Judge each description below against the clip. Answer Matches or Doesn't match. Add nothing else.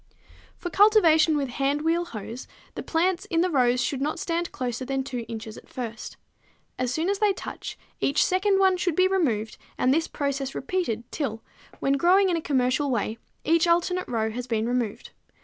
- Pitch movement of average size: Doesn't match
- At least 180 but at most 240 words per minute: Matches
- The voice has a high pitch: Matches